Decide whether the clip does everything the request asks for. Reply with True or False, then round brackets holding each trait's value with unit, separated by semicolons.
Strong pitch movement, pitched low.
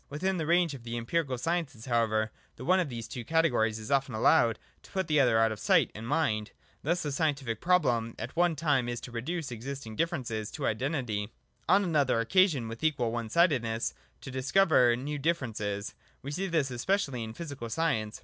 True (6.0 semitones; 130 Hz)